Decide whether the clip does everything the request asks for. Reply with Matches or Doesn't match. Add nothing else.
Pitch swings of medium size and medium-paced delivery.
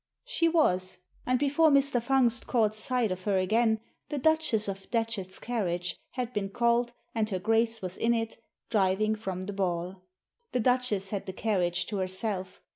Matches